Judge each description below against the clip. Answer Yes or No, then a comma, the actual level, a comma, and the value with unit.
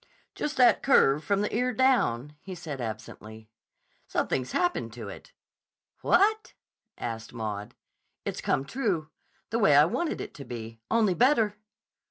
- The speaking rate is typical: Yes, average, 145 wpm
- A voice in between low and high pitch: Yes, medium, 160 Hz